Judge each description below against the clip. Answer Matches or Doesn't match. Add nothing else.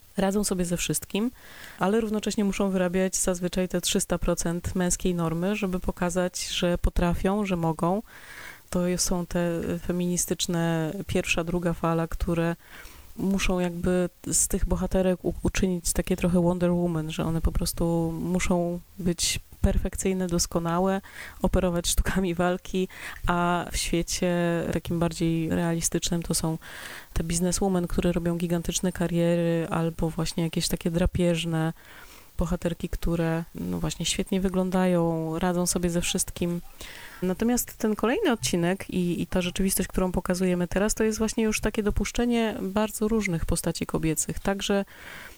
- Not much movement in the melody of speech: Matches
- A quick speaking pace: Doesn't match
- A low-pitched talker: Doesn't match